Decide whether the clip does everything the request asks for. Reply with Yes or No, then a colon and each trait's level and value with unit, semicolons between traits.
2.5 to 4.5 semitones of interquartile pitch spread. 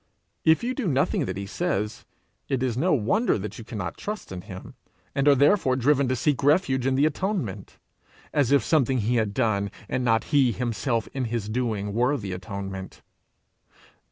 No: average, 5.2 semitones